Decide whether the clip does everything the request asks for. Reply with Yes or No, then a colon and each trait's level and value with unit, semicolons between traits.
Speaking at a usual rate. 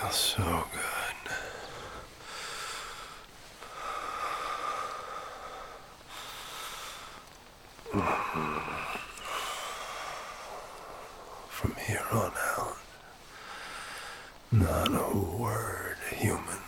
No: slow, 45 wpm